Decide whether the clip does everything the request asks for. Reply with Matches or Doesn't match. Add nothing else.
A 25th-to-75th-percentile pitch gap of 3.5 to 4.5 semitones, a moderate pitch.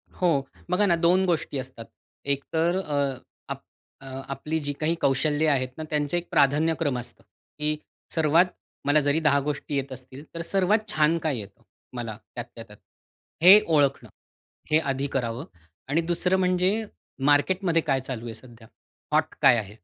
Matches